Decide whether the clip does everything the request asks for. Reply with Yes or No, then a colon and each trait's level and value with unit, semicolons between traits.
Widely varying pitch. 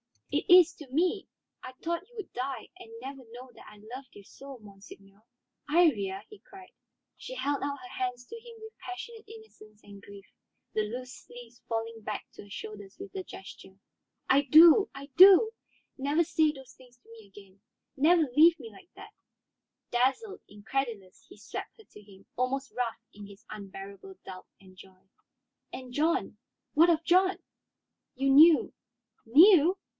Yes: wide, 8.2 semitones